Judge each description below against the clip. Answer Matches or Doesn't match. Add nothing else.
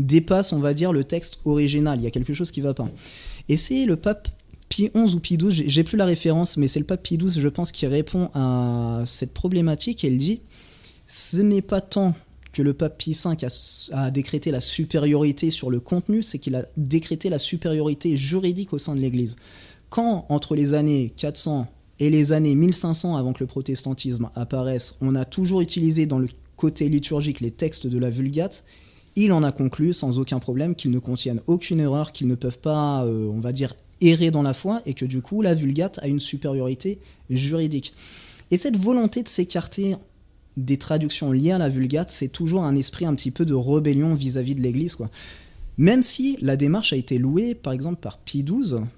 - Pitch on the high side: Doesn't match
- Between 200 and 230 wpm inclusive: Matches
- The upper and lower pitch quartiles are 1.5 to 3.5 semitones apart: Doesn't match